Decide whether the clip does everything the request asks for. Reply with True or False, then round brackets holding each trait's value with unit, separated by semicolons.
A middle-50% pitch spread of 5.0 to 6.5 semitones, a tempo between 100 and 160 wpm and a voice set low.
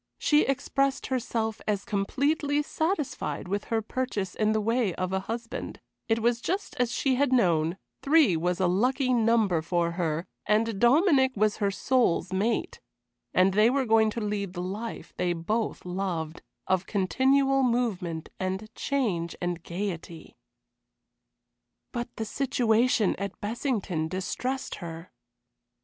False (5.5 semitones; 140 wpm; 215 Hz)